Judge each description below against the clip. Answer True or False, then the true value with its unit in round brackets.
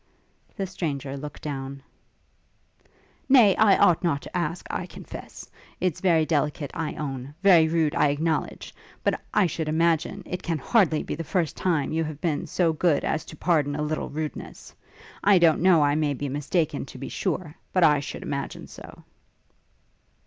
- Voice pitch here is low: False (155 Hz)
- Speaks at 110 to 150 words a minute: False (175 wpm)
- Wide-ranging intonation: False (3.1 semitones)